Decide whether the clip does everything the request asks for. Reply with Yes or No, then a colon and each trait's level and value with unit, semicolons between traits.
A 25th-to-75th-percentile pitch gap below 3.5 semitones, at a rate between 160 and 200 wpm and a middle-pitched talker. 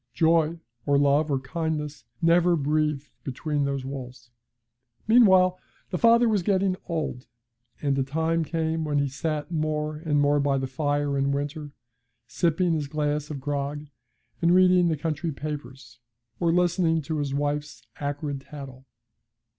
No: average, 2.7 semitones; average, 145 wpm; medium, 150 Hz